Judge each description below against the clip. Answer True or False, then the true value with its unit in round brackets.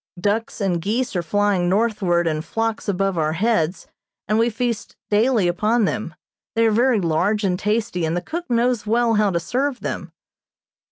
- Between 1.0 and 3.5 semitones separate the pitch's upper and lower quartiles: False (4.5 semitones)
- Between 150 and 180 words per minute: True (175 wpm)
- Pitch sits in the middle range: False (210 Hz)